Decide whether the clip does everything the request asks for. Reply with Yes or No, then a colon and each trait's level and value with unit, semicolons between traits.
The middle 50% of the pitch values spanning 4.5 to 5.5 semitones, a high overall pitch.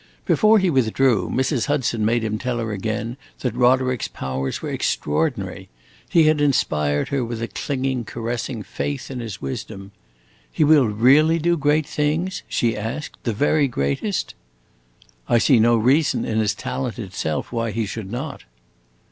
No: average, 4.8 semitones; low, 120 Hz